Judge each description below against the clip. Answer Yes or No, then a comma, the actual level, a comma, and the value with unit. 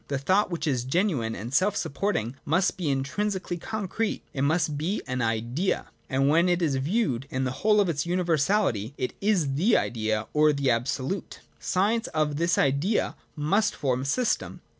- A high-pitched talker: No, medium, 150 Hz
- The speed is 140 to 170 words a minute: No, average, 185 wpm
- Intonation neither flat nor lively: No, wide, 6.2 semitones